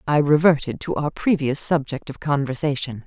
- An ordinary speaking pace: Yes, average, 155 wpm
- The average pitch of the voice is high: No, medium, 145 Hz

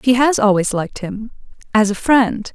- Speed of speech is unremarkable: Yes, average, 165 wpm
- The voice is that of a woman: Yes, female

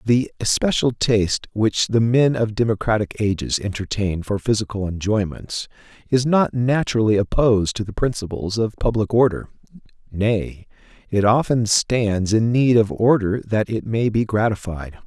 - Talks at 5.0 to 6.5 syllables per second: No, 4.7 syllables/s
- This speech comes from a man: Yes, male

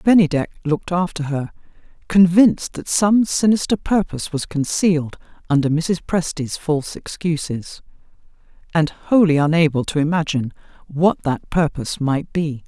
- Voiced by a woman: Yes, female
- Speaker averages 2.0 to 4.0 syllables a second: No, 4.9 syllables/s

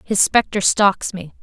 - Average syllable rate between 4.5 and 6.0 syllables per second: No, 3.9 syllables/s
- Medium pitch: No, high, 195 Hz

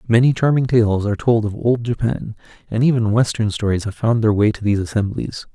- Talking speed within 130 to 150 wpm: No, fast, 205 wpm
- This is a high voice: No, low, 110 Hz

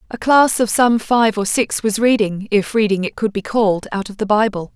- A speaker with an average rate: No, fast, 240 wpm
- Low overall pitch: No, high, 215 Hz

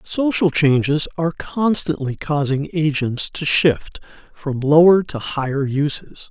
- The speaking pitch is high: No, medium, 150 Hz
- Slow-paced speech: Yes, slow, 125 wpm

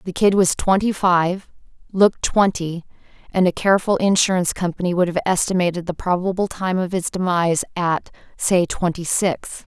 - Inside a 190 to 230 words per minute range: No, average, 155 wpm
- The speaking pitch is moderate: Yes, medium, 180 Hz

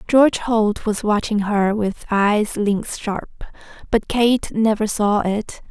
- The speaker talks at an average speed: Yes, average, 145 wpm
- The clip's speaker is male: No, female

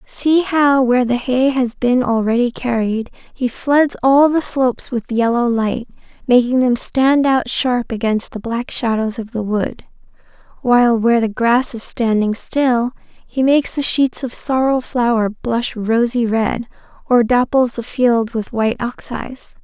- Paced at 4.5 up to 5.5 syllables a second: No, 4.2 syllables/s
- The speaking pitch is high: Yes, high, 245 Hz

